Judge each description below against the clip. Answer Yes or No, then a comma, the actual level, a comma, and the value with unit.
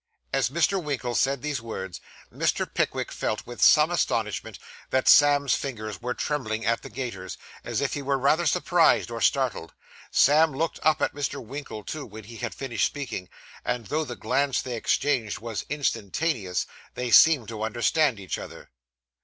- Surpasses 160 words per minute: Yes, average, 170 wpm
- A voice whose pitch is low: Yes, low, 130 Hz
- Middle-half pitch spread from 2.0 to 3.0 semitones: No, average, 4.3 semitones